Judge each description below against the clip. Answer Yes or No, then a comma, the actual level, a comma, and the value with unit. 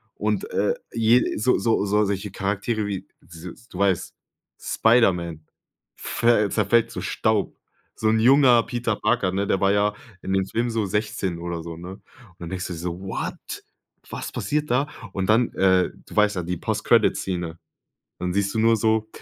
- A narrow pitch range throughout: No, average, 3.7 semitones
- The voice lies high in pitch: No, low, 100 Hz